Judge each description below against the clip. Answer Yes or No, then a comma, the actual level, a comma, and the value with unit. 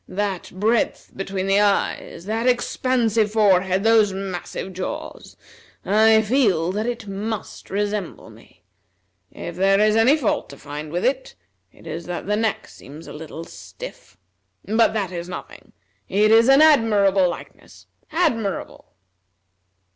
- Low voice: No, high, 205 Hz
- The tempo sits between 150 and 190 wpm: No, average, 140 wpm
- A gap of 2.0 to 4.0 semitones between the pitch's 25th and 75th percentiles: Yes, average, 3.2 semitones